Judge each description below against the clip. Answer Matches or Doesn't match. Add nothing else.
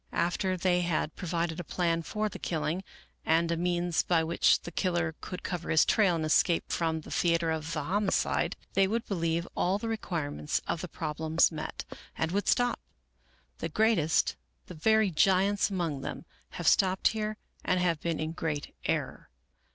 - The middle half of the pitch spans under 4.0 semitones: Matches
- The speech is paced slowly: Doesn't match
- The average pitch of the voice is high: Doesn't match